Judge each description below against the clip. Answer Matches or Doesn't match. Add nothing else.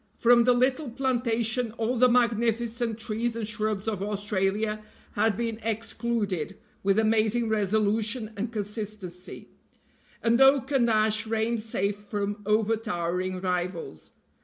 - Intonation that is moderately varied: Doesn't match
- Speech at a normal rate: Doesn't match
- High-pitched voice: Matches